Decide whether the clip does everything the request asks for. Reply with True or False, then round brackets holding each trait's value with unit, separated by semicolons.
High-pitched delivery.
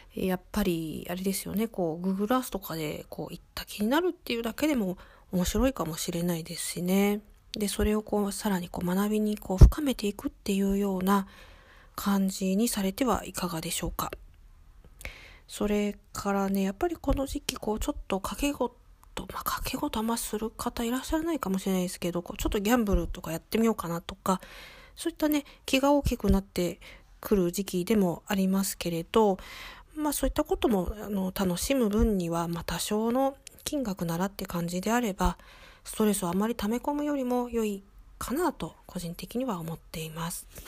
True (200 Hz)